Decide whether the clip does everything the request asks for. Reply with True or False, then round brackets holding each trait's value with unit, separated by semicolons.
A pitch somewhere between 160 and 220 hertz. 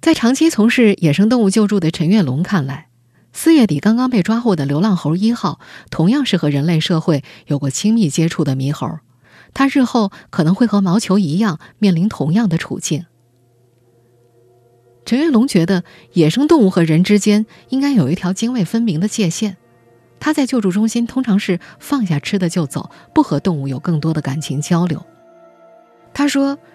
True (185 Hz)